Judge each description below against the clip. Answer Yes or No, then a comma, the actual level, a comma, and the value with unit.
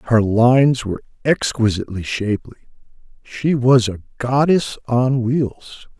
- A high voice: No, low, 120 Hz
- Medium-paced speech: No, slow, 110 wpm